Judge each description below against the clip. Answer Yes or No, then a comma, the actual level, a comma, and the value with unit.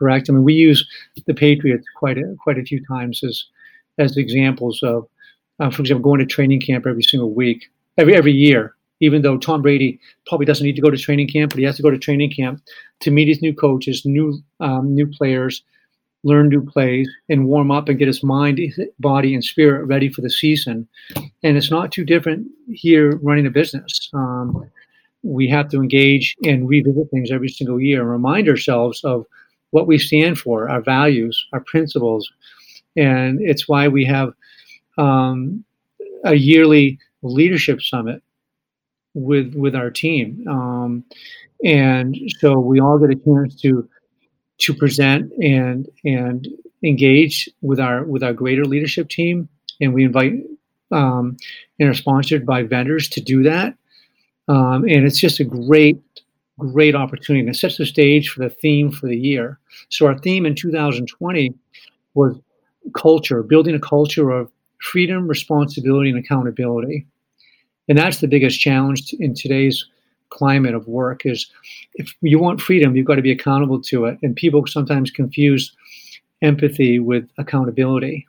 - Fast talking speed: No, average, 170 wpm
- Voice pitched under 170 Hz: Yes, medium, 140 Hz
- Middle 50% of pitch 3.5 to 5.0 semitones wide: No, narrow, 2.5 semitones